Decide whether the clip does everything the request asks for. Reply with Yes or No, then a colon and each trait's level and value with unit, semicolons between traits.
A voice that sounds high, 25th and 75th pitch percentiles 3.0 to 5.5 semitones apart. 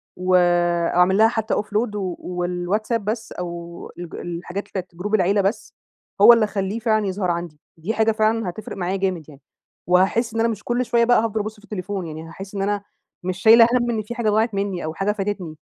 Yes: high, 200 Hz; average, 3.6 semitones